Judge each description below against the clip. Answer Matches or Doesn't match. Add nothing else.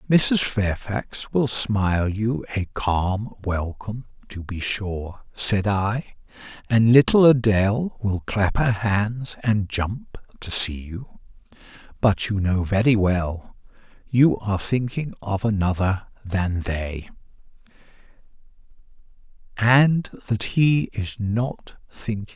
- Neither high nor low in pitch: Doesn't match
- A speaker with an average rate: Doesn't match